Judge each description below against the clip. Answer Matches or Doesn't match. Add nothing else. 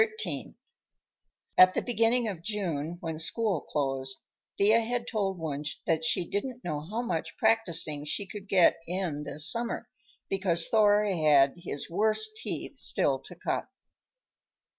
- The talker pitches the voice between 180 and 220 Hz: Matches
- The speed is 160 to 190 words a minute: Doesn't match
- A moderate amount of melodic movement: Doesn't match